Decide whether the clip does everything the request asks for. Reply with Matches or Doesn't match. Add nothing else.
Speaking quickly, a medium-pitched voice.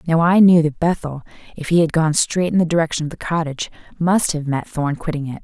Matches